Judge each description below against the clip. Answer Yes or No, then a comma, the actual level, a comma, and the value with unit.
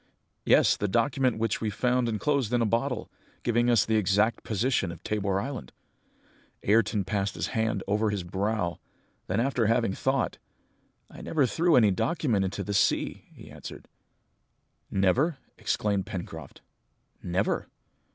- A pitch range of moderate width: Yes, average, 3.9 semitones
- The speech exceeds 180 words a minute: No, average, 140 wpm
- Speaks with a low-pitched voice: Yes, low, 110 Hz